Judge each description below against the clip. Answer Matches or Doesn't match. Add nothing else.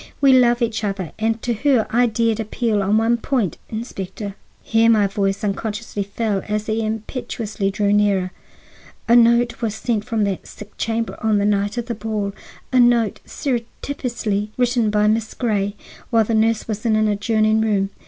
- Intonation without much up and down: Matches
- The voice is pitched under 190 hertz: Doesn't match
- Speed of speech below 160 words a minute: Doesn't match